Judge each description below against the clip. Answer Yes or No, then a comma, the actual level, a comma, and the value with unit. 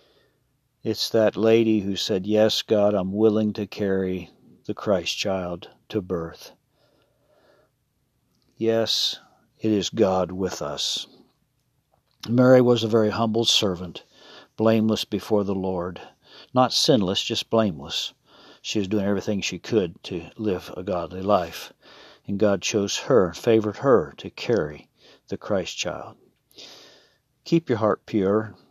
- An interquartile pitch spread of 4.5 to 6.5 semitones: No, average, 2.9 semitones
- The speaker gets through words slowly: Yes, slow, 130 wpm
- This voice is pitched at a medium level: No, low, 105 Hz